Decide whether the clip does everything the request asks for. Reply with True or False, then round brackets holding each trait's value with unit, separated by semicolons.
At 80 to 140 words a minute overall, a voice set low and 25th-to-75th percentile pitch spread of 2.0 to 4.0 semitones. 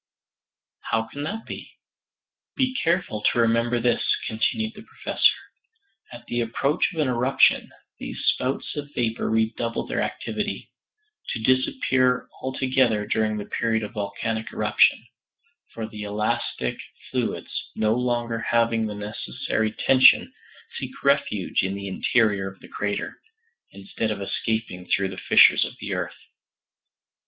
True (135 wpm; 115 Hz; 3.1 semitones)